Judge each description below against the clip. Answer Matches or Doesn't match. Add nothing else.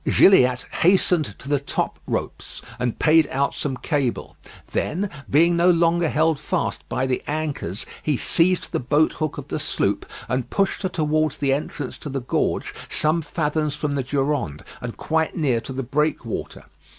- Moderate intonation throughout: Matches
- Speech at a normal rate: Matches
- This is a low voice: Doesn't match